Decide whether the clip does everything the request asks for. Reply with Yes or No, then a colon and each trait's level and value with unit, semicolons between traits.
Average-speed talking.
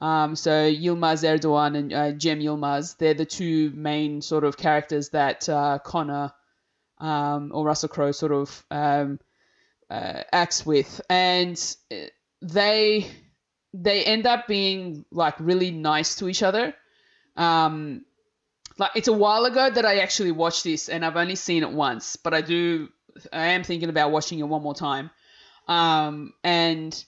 Yes: average, 155 wpm